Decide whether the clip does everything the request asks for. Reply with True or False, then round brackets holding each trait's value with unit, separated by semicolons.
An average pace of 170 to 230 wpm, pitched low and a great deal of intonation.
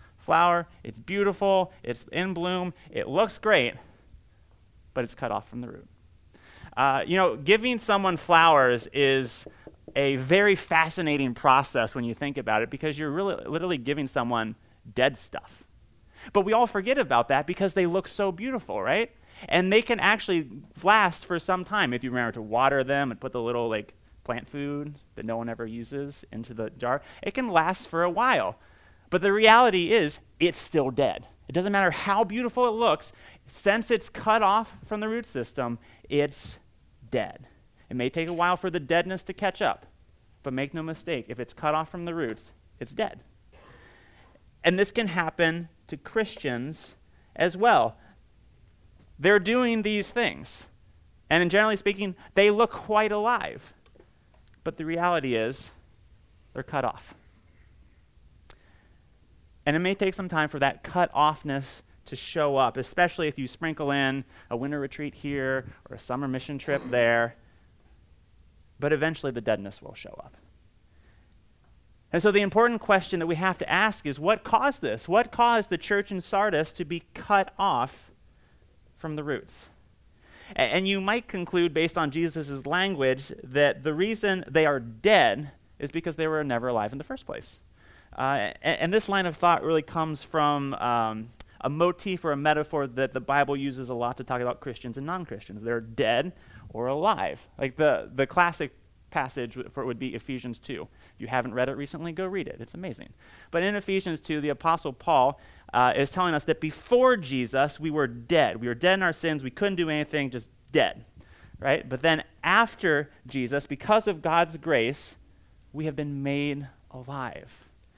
False (175 wpm; 150 Hz; 7.0 semitones)